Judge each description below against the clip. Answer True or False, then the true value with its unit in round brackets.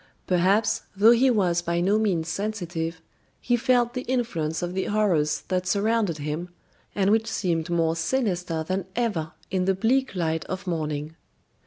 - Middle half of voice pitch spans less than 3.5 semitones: False (4.8 semitones)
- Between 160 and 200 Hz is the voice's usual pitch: True (185 Hz)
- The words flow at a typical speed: True (160 wpm)